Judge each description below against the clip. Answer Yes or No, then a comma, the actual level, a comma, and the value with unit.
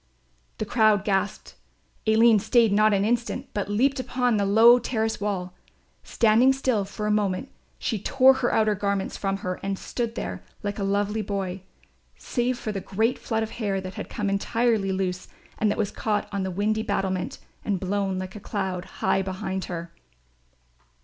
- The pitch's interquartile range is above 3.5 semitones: No, narrow, 2.6 semitones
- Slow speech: No, average, 175 wpm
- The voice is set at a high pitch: Yes, high, 205 Hz